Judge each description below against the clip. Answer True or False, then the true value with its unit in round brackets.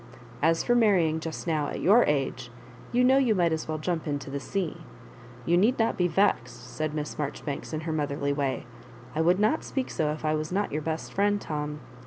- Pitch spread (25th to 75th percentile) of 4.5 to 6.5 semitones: True (4.8 semitones)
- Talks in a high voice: False (160 Hz)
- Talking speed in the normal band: False (215 wpm)